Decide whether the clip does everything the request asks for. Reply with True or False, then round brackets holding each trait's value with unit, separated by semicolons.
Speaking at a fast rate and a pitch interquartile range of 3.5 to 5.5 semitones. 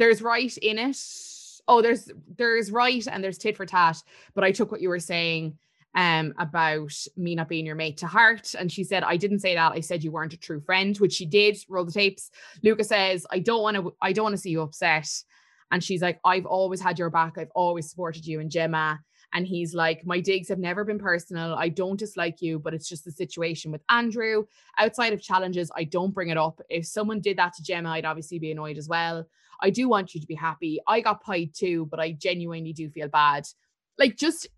True (230 wpm; 4.1 semitones)